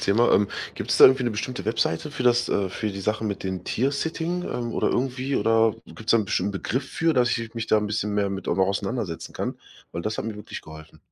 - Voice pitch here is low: Yes, low, 110 Hz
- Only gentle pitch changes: No, average, 3.8 semitones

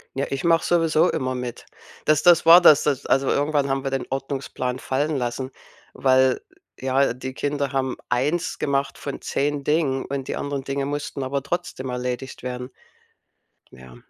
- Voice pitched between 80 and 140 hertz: Yes, low, 135 Hz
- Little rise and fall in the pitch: Yes, narrow, 2.0 semitones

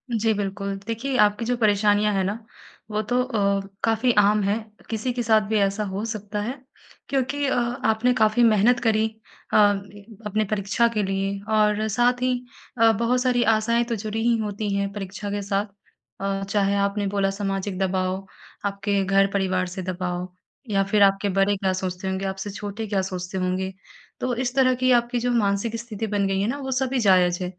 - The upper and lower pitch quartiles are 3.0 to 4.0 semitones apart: No, narrow, 2.5 semitones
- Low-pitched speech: No, high, 205 Hz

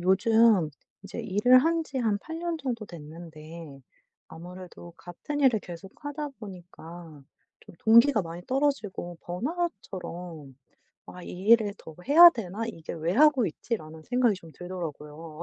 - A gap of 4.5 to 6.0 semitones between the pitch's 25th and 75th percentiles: No, wide, 6.7 semitones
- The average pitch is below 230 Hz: Yes, high, 190 Hz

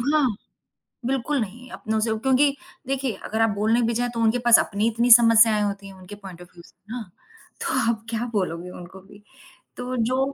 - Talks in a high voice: Yes, high, 225 Hz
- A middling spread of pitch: Yes, average, 3.5 semitones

